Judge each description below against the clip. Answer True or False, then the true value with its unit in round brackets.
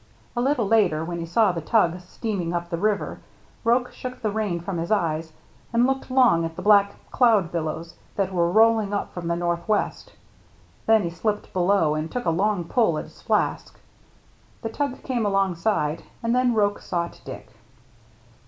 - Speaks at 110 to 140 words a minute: False (180 wpm)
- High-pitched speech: True (195 Hz)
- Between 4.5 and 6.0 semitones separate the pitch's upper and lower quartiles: True (4.8 semitones)